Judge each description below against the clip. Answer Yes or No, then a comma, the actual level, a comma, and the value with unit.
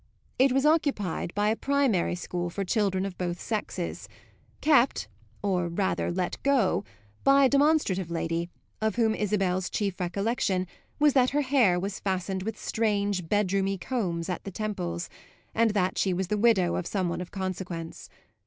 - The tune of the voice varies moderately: Yes, average, 4.0 semitones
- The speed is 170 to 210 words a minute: No, average, 160 wpm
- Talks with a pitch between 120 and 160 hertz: No, high, 195 Hz